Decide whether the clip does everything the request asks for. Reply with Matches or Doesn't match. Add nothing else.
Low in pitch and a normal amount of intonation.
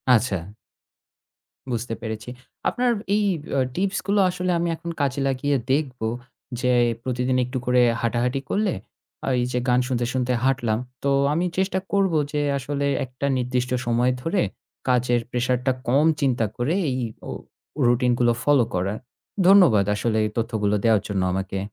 Matches